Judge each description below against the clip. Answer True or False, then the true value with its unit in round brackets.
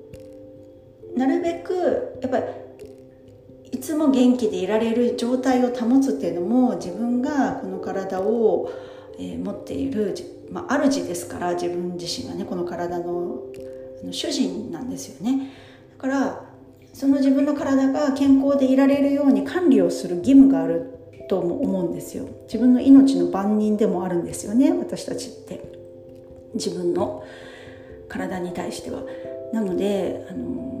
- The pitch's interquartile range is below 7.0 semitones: False (7.7 semitones)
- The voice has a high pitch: True (235 Hz)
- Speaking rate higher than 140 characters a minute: True (270 characters per minute)